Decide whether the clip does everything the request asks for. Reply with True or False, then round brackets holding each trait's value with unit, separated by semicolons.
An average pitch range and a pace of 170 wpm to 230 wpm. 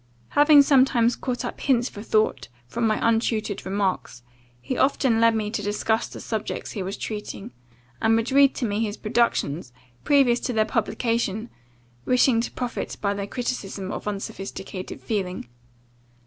False (3.1 semitones; 155 wpm)